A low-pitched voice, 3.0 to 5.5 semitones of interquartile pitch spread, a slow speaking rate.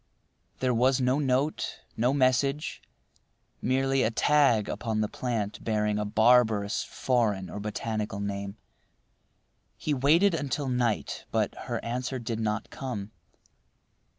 Yes: low, 120 Hz; average, 3.8 semitones; slow, 125 wpm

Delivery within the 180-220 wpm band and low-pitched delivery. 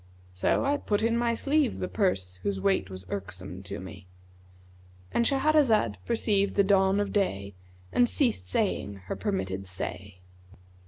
No: average, 145 wpm; low, 100 Hz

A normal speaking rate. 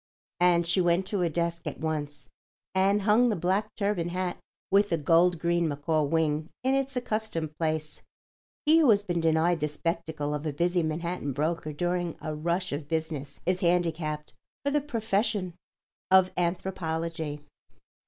Yes: average, 160 wpm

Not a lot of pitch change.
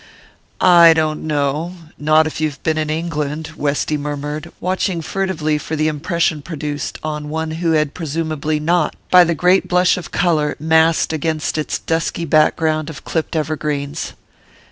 Yes: narrow, 1.6 semitones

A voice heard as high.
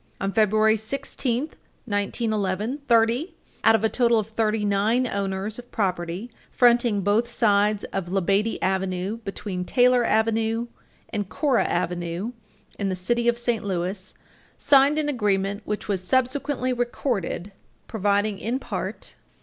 Yes: high, 215 Hz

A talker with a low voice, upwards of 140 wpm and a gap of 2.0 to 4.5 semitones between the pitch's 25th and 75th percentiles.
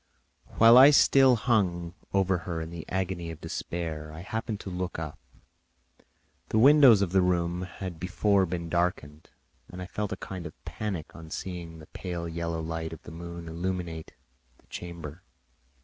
Yes: very low, 85 Hz; average, 165 wpm; narrow, 2.6 semitones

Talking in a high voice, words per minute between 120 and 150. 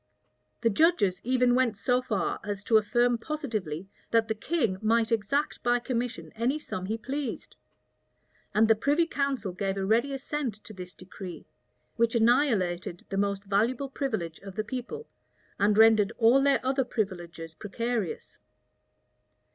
Yes: high, 225 Hz; average, 145 wpm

